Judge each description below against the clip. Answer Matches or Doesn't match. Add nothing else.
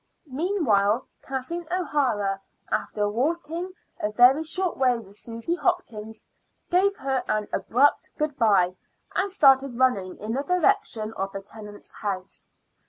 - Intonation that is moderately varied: Doesn't match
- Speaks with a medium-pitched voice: Doesn't match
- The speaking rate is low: Matches